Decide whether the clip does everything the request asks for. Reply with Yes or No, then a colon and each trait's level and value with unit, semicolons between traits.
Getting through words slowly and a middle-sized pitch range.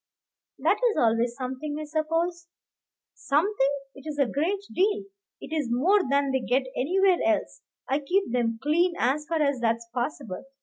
No: average, 165 wpm; average, 5.0 semitones